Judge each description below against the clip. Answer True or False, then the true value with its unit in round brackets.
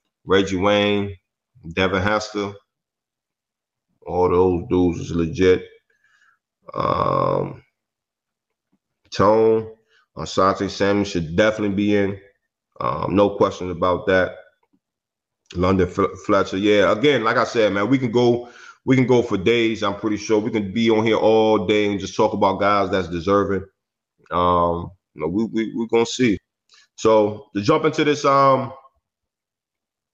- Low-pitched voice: True (100 Hz)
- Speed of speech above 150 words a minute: False (140 wpm)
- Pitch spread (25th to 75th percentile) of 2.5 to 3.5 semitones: True (2.8 semitones)